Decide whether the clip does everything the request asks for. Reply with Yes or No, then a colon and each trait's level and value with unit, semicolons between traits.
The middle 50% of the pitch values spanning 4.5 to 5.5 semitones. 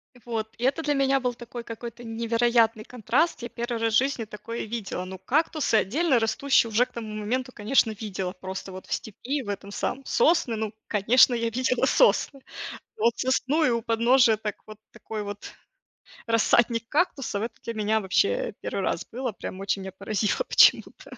No: average, 3.1 semitones